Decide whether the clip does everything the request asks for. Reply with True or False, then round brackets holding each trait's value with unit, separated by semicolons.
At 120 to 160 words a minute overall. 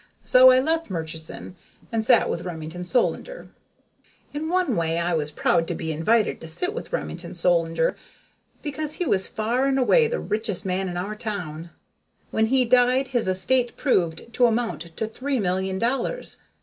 False (170 wpm)